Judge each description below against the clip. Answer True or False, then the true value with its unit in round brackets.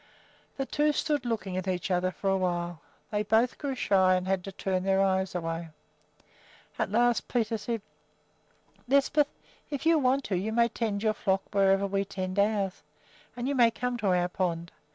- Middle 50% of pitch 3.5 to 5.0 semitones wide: True (4.3 semitones)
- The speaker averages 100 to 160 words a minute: False (185 wpm)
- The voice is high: True (200 Hz)